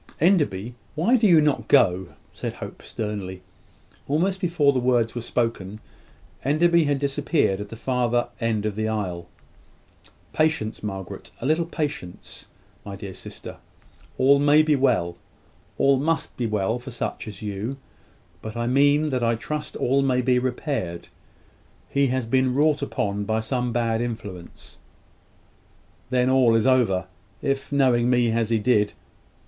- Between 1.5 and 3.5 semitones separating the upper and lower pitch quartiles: No, average, 4.6 semitones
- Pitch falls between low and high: No, low, 125 Hz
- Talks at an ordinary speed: Yes, average, 155 wpm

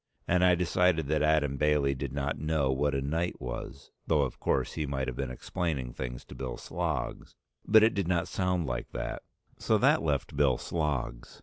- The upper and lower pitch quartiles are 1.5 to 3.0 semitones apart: No, average, 4.0 semitones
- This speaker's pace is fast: No, average, 195 wpm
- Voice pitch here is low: Yes, very low, 75 Hz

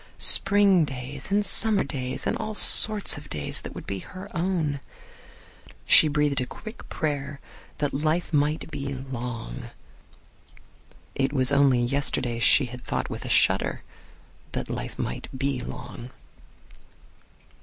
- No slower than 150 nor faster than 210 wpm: No, slow, 135 wpm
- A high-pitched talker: No, medium, 140 Hz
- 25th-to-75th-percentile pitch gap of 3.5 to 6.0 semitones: Yes, average, 4.2 semitones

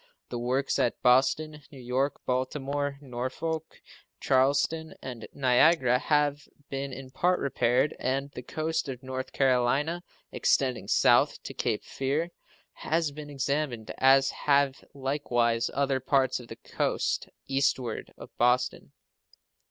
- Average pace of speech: No, slow, 125 wpm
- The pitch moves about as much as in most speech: No, narrow, 2.3 semitones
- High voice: No, low, 135 Hz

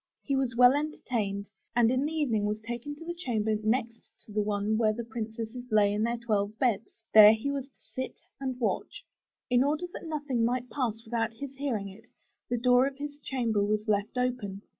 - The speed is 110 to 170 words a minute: No, fast, 205 wpm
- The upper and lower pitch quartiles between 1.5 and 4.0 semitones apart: Yes, average, 3.6 semitones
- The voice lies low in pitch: No, high, 235 Hz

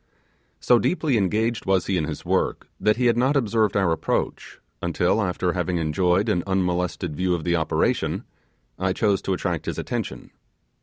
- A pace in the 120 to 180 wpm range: Yes, average, 170 wpm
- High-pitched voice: No, very low, 95 Hz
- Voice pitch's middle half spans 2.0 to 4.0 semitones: Yes, average, 3.4 semitones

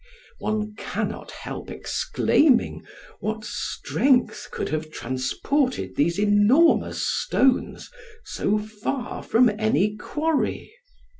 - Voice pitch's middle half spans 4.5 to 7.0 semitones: No, average, 4.1 semitones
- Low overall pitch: No, high, 215 Hz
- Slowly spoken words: Yes, slow, 90 wpm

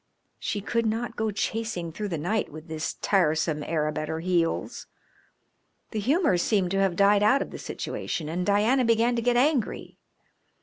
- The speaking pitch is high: Yes, high, 200 Hz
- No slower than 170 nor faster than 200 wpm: Yes, average, 175 wpm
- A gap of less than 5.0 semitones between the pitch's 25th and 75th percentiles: No, wide, 5.4 semitones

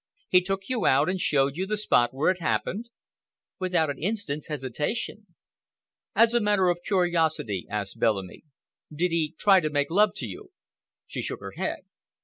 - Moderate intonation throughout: No, wide, 6.0 semitones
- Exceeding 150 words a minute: Yes, average, 170 wpm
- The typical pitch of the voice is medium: Yes, medium, 175 Hz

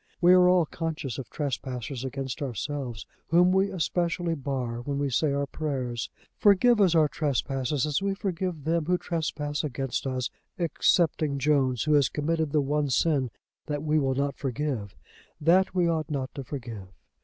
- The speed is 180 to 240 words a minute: No, average, 165 wpm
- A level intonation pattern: No, average, 3.8 semitones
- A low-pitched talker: No, medium, 145 Hz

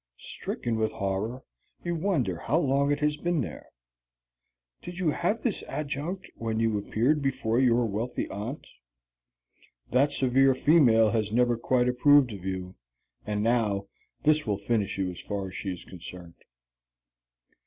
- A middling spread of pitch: No, wide, 5.8 semitones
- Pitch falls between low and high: No, low, 120 Hz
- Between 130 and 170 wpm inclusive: Yes, average, 150 wpm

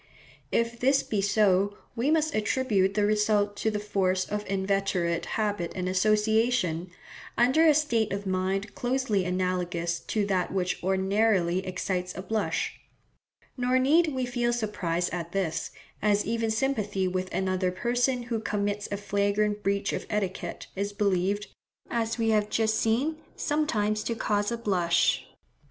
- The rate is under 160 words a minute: Yes, average, 145 wpm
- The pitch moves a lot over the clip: No, average, 3.3 semitones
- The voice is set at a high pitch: Yes, high, 205 Hz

